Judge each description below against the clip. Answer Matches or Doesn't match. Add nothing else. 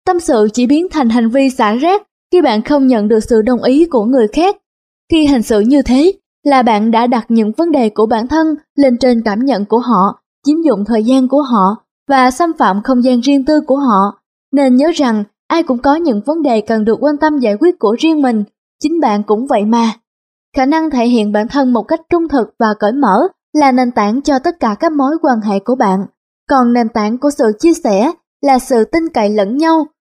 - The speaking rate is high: Doesn't match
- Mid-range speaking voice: Doesn't match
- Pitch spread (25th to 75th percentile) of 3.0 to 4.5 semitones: Doesn't match